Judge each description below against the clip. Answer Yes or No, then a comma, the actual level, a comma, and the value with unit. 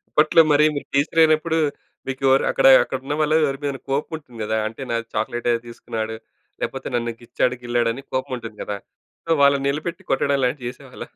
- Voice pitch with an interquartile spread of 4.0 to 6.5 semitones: No, average, 3.5 semitones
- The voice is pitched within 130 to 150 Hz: Yes, low, 135 Hz